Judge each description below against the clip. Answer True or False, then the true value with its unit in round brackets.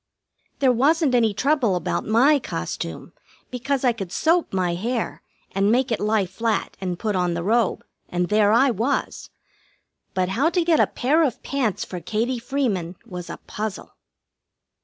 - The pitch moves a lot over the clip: True (5.8 semitones)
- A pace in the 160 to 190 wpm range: True (165 wpm)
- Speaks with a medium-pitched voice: False (225 Hz)